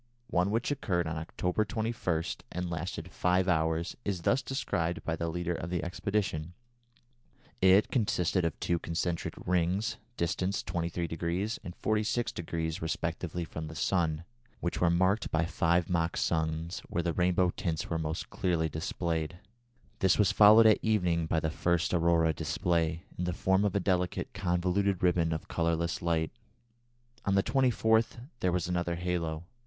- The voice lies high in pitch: No, very low, 85 Hz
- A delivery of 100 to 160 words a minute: Yes, average, 155 wpm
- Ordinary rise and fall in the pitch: No, narrow, 2.3 semitones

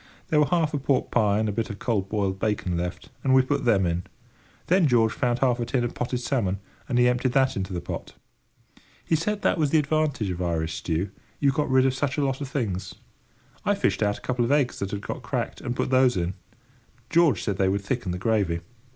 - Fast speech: Yes, fast, 235 wpm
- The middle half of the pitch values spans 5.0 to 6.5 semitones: Yes, wide, 5.6 semitones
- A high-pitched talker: No, low, 120 Hz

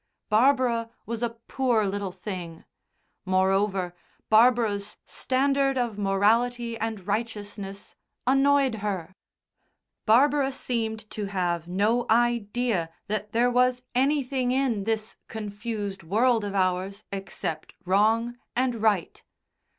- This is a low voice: No, high, 220 Hz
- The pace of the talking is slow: Yes, slow, 105 wpm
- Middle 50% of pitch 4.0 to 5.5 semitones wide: No, average, 3.6 semitones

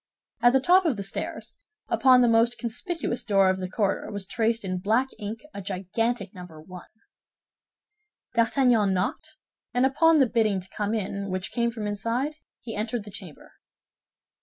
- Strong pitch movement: No, average, 3.8 semitones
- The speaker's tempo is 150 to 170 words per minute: Yes, average, 165 wpm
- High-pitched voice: Yes, high, 220 Hz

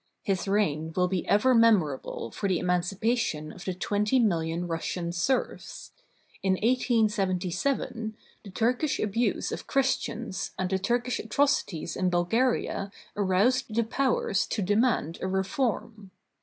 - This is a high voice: Yes, high, 200 Hz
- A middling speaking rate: No, slow, 130 wpm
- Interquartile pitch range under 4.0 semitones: No, average, 4.5 semitones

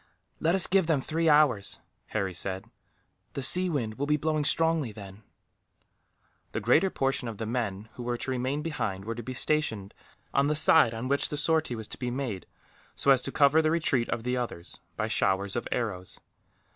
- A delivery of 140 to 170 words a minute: No, average, 195 wpm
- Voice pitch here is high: No, low, 125 Hz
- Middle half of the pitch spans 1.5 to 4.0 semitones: No, wide, 5.5 semitones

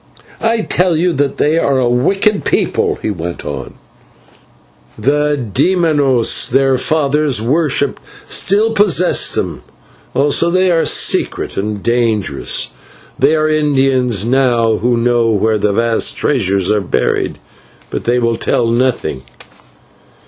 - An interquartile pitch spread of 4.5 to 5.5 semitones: Yes, average, 5.1 semitones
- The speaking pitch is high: No, low, 130 Hz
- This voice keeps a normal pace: No, slow, 125 wpm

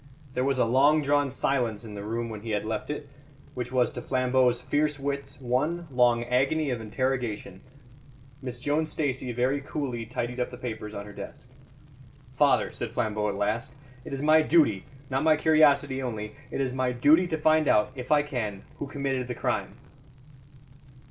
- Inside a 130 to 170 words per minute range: No, average, 180 wpm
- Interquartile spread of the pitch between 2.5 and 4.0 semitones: Yes, average, 3.4 semitones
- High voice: No, low, 130 Hz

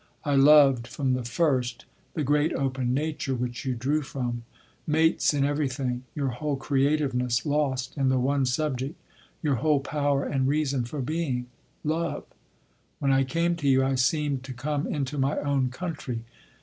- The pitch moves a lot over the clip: No, narrow, 2.6 semitones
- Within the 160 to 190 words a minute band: No, average, 150 wpm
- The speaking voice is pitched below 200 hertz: Yes, low, 135 Hz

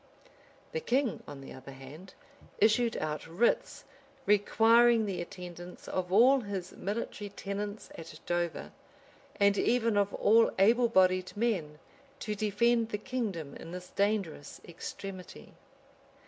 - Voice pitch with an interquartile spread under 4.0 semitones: No, average, 4.3 semitones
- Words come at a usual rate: No, slow, 125 wpm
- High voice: Yes, high, 200 Hz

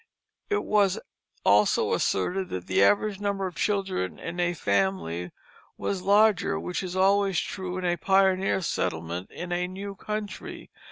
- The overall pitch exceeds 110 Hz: Yes, medium, 185 Hz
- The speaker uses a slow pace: No, average, 150 wpm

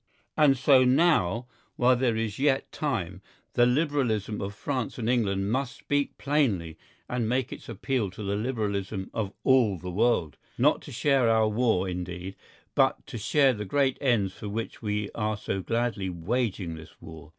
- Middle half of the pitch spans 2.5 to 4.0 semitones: No, average, 4.8 semitones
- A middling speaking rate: Yes, average, 170 wpm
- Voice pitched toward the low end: Yes, low, 110 Hz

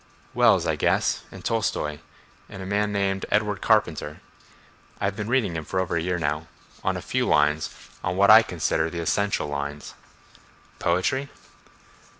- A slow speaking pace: No, average, 150 wpm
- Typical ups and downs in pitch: Yes, average, 4.4 semitones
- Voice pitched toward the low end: Yes, very low, 90 Hz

